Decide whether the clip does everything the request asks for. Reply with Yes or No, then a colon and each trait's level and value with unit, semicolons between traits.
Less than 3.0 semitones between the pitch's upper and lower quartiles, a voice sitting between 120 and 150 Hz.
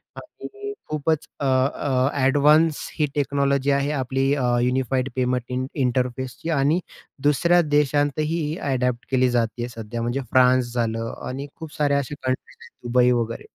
Yes: narrow, 2.5 semitones; low, 135 Hz